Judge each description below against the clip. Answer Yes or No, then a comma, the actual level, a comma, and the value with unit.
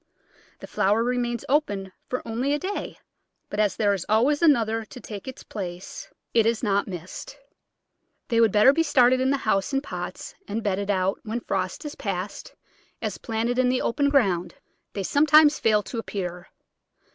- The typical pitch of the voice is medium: No, high, 225 Hz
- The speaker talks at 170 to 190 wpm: Yes, average, 175 wpm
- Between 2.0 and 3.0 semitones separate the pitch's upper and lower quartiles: No, average, 4.7 semitones